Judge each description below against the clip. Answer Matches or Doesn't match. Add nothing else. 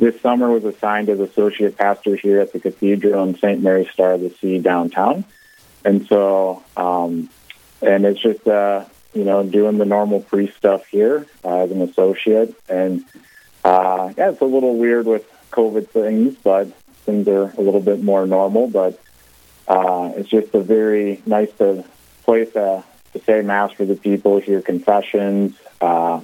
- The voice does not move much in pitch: Matches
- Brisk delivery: Doesn't match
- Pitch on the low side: Matches